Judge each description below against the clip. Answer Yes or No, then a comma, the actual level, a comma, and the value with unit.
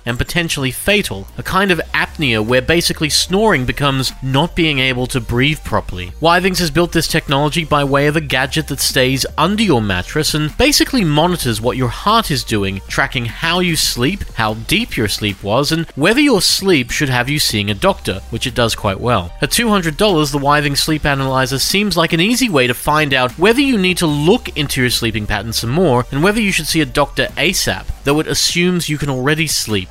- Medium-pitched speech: Yes, medium, 145 Hz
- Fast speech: Yes, fast, 210 wpm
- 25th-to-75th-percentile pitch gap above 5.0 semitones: Yes, wide, 5.6 semitones